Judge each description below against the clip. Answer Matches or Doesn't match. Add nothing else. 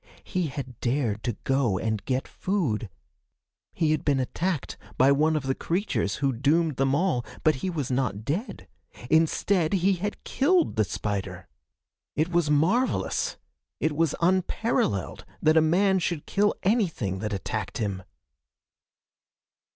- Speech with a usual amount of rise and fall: Doesn't match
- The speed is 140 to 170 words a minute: Matches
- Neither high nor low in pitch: Matches